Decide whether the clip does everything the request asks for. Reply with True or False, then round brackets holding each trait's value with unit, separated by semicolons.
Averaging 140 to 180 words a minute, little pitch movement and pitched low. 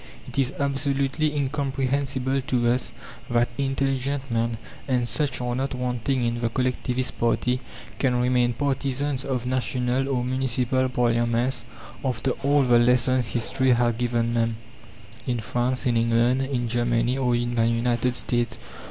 True (145 wpm; 1.9 semitones; 125 Hz)